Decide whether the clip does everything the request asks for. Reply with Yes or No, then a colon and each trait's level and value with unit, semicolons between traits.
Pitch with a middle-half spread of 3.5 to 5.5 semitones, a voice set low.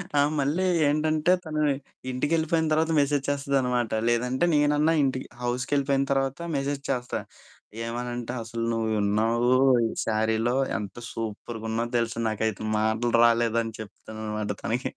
Yes: average, 4.0 semitones; low, 120 Hz